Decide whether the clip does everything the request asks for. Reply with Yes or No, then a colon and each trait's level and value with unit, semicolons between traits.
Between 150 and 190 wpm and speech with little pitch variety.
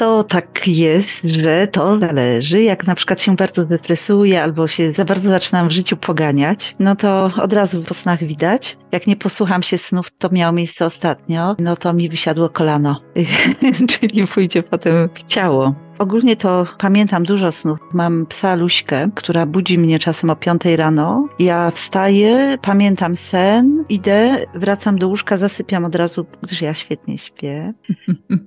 No: fast, 160 wpm; average, 3.1 semitones